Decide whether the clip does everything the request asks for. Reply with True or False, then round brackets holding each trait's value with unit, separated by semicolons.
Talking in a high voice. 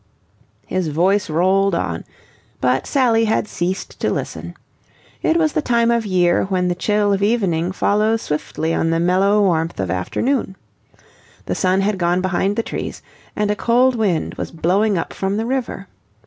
True (195 Hz)